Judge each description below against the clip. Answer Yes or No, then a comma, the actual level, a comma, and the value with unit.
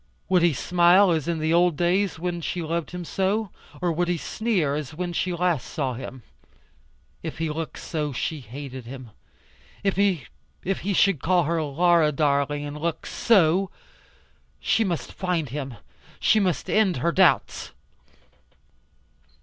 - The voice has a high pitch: No, medium, 170 Hz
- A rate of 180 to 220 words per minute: No, average, 150 wpm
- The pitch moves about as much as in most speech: Yes, average, 3.4 semitones